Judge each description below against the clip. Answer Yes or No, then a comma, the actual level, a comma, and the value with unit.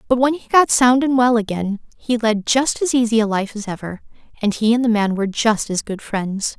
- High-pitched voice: Yes, high, 225 Hz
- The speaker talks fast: Yes, fast, 245 wpm